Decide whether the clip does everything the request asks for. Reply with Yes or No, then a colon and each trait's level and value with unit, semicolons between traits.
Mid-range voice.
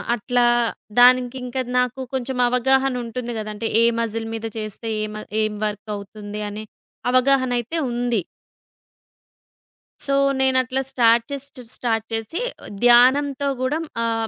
No: high, 245 Hz